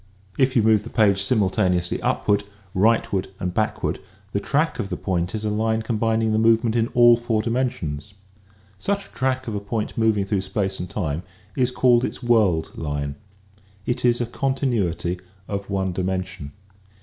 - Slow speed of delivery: No, average, 175 wpm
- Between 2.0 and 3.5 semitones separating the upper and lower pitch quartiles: No, average, 3.9 semitones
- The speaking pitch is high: No, low, 110 Hz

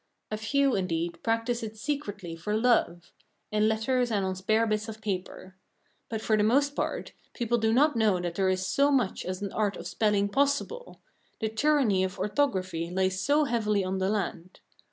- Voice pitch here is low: No, high, 215 Hz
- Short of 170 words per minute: No, average, 185 wpm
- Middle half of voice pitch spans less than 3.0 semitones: No, average, 4.1 semitones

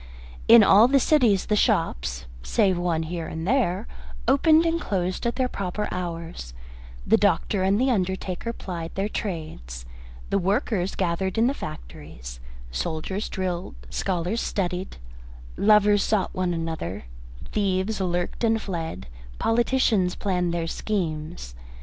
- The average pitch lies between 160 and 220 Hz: Yes, medium, 185 Hz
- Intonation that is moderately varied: Yes, average, 4.3 semitones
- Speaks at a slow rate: Yes, slow, 130 wpm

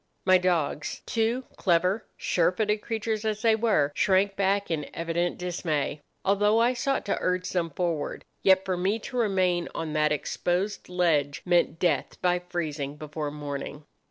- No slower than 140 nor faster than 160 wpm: Yes, average, 150 wpm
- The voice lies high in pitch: No, medium, 180 Hz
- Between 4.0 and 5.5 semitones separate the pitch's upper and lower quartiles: Yes, average, 4.3 semitones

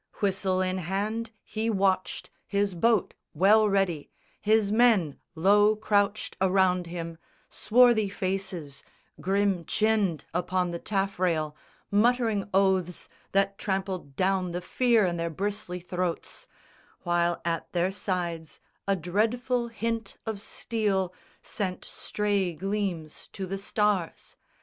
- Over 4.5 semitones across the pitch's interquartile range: No, average, 2.8 semitones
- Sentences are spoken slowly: Yes, slow, 115 wpm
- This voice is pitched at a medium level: No, high, 195 Hz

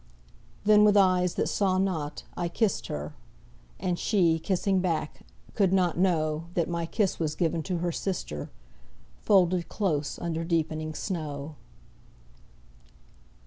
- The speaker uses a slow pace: Yes, slow, 130 wpm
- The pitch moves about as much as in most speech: Yes, average, 3.2 semitones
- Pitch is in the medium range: Yes, medium, 175 Hz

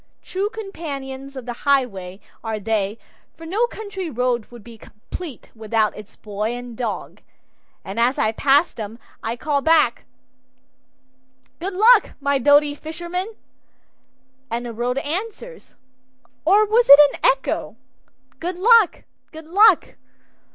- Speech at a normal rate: No, slow, 130 wpm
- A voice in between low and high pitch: No, very high, 275 Hz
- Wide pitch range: Yes, wide, 7.6 semitones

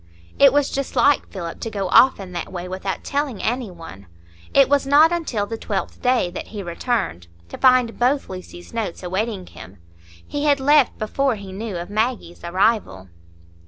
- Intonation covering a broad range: Yes, wide, 6.4 semitones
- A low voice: No, high, 220 Hz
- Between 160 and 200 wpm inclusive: Yes, average, 180 wpm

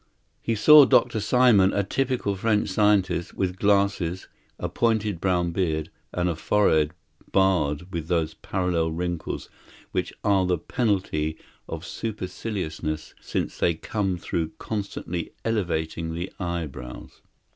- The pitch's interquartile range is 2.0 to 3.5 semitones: No, average, 3.9 semitones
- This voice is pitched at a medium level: No, very low, 90 Hz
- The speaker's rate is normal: No, slow, 125 wpm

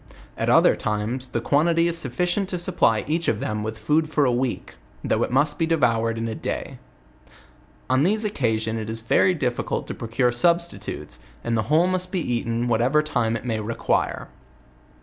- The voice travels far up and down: Yes, wide, 6.4 semitones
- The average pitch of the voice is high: No, low, 125 Hz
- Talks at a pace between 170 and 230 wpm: Yes, average, 190 wpm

